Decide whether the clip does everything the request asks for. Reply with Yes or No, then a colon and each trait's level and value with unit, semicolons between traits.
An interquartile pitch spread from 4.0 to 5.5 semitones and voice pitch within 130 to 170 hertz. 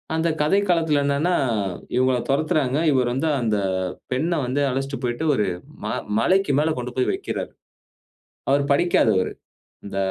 Yes: average, 4.4 semitones; medium, 140 Hz